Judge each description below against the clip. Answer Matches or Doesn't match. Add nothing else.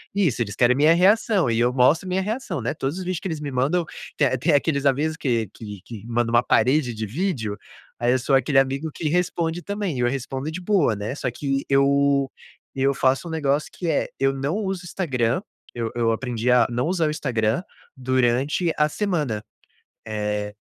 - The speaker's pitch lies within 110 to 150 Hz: Matches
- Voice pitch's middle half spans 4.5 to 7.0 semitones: Matches